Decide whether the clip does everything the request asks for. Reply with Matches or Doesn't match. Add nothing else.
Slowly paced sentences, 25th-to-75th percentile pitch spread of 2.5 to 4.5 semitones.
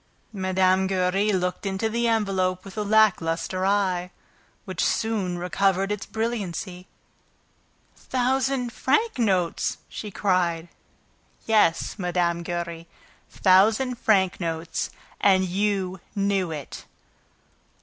Matches